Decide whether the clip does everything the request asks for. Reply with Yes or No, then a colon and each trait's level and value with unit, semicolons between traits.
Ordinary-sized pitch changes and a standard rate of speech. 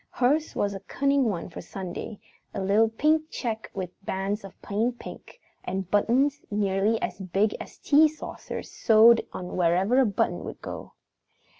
Yes: average, 4.5 semitones; average, 160 wpm